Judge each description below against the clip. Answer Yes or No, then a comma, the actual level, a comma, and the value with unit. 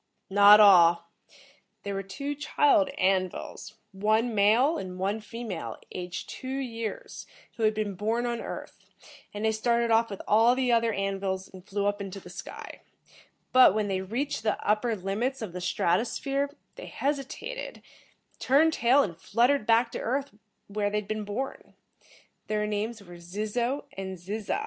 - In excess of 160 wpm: Yes, average, 170 wpm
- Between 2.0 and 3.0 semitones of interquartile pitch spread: No, average, 3.6 semitones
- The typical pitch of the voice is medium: No, high, 215 Hz